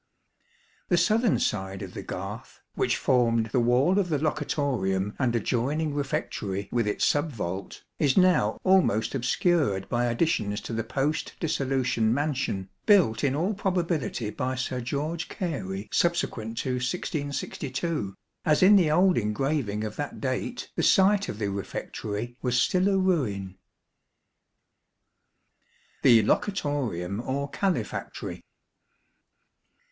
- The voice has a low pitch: Yes, low, 130 Hz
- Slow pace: Yes, slow, 125 wpm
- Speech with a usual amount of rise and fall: No, wide, 6.7 semitones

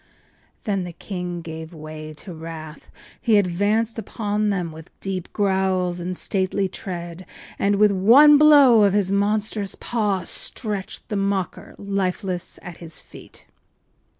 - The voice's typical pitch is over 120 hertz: Yes, high, 190 Hz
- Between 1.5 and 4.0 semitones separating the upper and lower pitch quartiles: Yes, average, 2.9 semitones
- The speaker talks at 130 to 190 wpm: Yes, average, 140 wpm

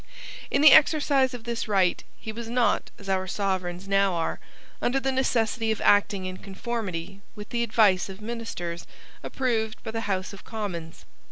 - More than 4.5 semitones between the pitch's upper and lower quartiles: No, average, 3.8 semitones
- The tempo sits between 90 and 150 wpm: No, average, 170 wpm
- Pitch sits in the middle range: No, high, 210 Hz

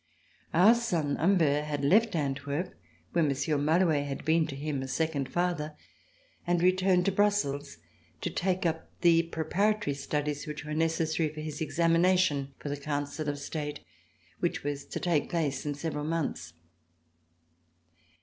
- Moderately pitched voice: Yes, medium, 155 Hz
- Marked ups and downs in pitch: No, average, 3.2 semitones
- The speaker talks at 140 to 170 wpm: Yes, average, 150 wpm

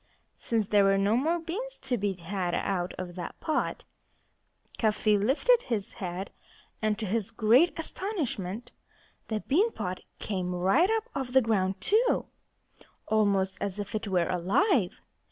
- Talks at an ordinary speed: Yes, average, 150 wpm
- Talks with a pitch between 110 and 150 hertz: No, high, 215 Hz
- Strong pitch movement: Yes, wide, 5.9 semitones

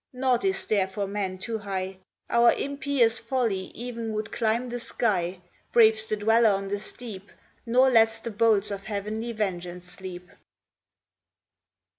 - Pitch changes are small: No, average, 3.2 semitones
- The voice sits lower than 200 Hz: No, high, 220 Hz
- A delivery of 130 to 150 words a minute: Yes, average, 145 wpm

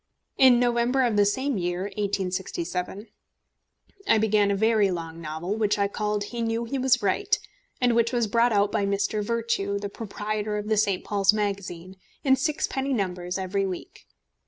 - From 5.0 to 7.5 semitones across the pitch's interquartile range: No, average, 3.1 semitones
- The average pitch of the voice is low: No, high, 210 Hz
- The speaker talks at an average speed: Yes, average, 170 wpm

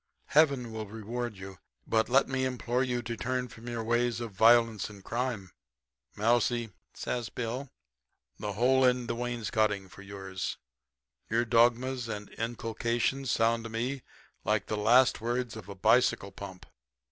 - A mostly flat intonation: Yes, narrow, 2.3 semitones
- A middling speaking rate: Yes, average, 150 wpm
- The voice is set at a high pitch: No, low, 115 Hz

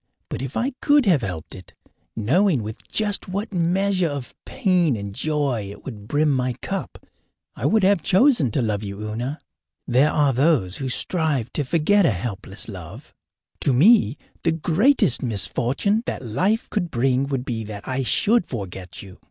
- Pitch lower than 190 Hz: Yes, medium, 140 Hz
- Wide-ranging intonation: Yes, wide, 8.2 semitones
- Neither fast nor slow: Yes, average, 170 wpm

